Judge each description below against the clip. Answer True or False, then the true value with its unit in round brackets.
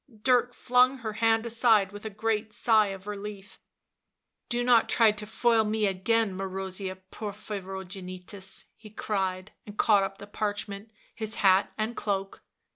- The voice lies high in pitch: True (210 Hz)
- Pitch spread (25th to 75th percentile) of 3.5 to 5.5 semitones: False (2.4 semitones)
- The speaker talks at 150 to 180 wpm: True (155 wpm)